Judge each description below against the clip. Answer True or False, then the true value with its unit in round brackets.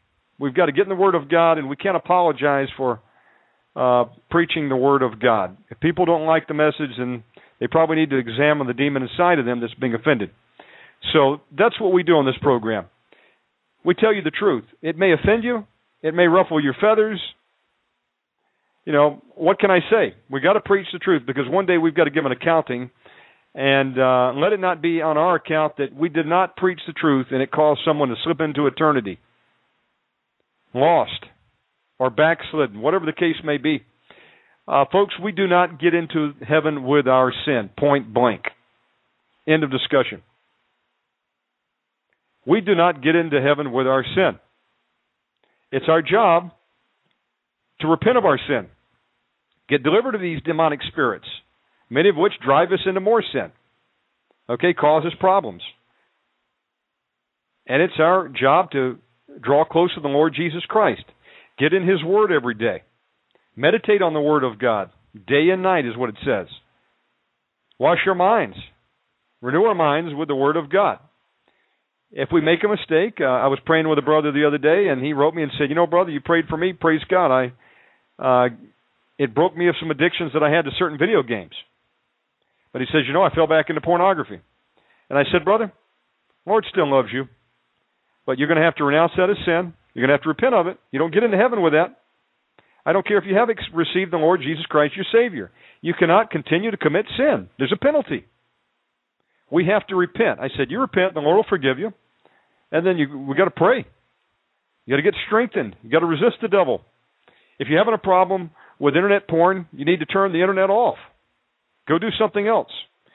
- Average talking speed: True (195 wpm)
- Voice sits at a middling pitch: True (160 Hz)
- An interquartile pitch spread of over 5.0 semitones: False (4.6 semitones)